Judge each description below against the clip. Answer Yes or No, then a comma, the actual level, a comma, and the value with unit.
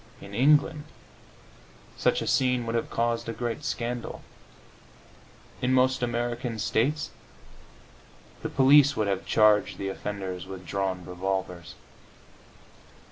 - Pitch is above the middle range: No, low, 115 Hz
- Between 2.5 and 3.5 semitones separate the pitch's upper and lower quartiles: No, average, 4.5 semitones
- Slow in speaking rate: Yes, slow, 115 wpm